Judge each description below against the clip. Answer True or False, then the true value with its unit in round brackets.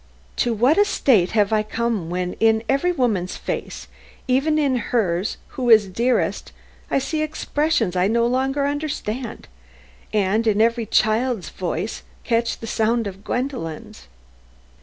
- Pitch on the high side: True (230 Hz)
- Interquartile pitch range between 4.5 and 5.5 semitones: False (4.1 semitones)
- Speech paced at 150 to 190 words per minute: False (140 wpm)